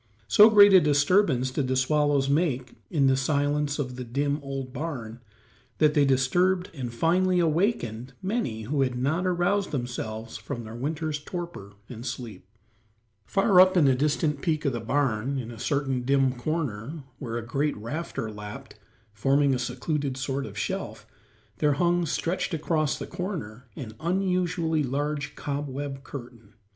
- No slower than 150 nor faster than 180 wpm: Yes, average, 155 wpm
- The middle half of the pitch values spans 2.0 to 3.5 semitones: No, average, 4.5 semitones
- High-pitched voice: No, medium, 140 Hz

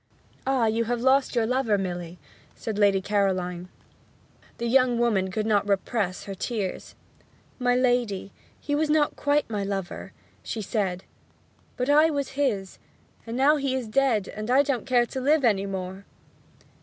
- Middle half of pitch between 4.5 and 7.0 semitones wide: Yes, average, 5.1 semitones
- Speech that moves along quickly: No, average, 155 wpm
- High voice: Yes, high, 230 Hz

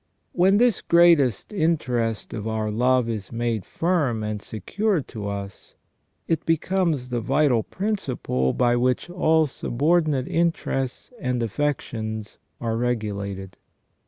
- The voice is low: Yes, low, 125 Hz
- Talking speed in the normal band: No, slow, 125 wpm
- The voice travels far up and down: Yes, wide, 6.8 semitones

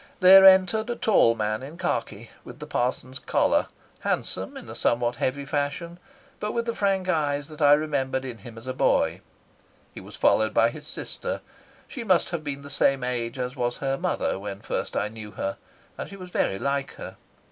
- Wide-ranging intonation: Yes, wide, 6.5 semitones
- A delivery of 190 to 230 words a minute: Yes, average, 200 wpm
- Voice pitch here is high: No, medium, 140 Hz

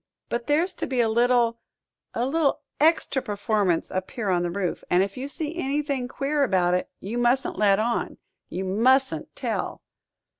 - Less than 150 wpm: No, average, 175 wpm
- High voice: Yes, high, 240 Hz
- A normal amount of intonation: No, wide, 5.7 semitones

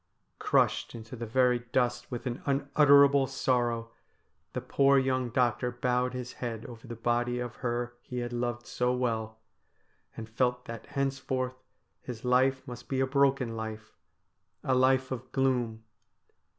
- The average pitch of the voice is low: Yes, low, 125 Hz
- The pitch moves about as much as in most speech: No, narrow, 1.6 semitones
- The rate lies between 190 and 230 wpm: No, average, 150 wpm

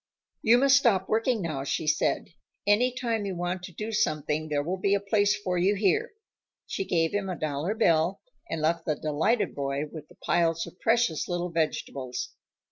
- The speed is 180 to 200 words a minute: Yes, average, 190 wpm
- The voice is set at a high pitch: No, medium, 180 Hz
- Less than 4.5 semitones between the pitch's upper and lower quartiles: No, average, 5.0 semitones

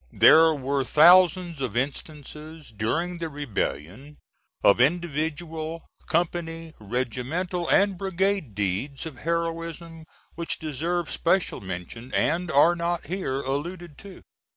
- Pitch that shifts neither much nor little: Yes, average, 4.2 semitones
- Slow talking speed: Yes, slow, 110 wpm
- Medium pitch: Yes, medium, 160 Hz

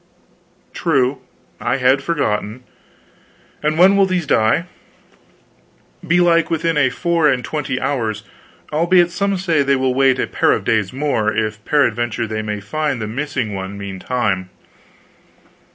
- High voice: No, low, 135 Hz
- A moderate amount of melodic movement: No, wide, 6.7 semitones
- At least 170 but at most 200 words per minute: No, slow, 135 wpm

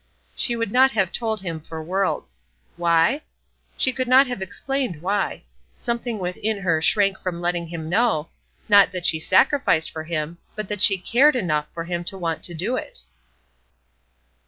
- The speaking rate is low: No, average, 170 wpm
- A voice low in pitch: No, high, 190 Hz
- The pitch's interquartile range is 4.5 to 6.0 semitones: Yes, wide, 5.4 semitones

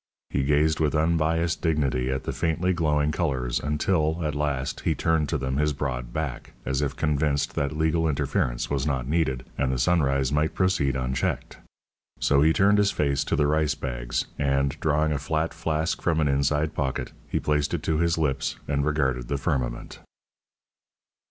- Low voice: Yes, very low, 75 Hz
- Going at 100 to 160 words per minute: No, average, 175 wpm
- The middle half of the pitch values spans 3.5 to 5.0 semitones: No, average, 2.7 semitones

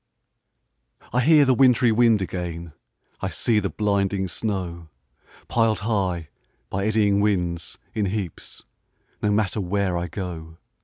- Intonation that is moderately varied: Yes, average, 3.6 semitones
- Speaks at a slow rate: Yes, slow, 125 wpm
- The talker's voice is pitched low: Yes, low, 100 Hz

